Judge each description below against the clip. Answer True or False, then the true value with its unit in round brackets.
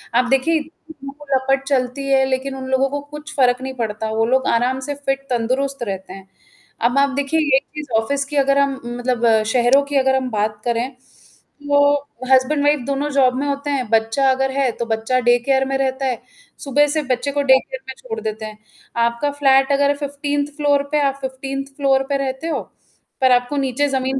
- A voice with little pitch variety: True (2.2 semitones)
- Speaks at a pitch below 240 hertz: False (270 Hz)